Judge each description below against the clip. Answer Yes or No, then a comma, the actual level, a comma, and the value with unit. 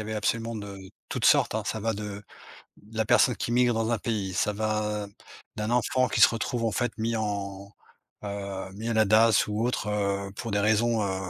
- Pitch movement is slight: Yes, narrow, 2.1 semitones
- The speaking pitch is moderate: No, low, 105 Hz